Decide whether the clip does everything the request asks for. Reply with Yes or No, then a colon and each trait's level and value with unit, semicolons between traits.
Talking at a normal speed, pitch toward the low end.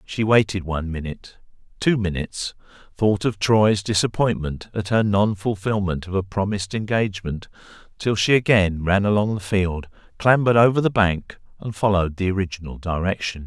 Yes: average, 145 wpm; low, 100 Hz